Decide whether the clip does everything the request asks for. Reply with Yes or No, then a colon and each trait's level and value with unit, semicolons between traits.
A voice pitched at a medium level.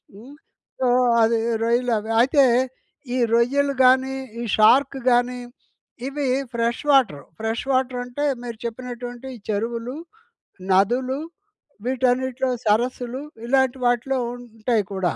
No: high, 245 Hz